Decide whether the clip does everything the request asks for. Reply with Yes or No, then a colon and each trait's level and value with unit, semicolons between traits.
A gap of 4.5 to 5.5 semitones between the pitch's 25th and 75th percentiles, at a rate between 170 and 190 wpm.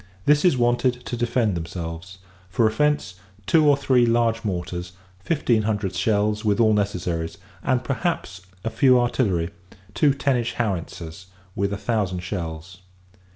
No: average, 5.0 semitones; average, 145 wpm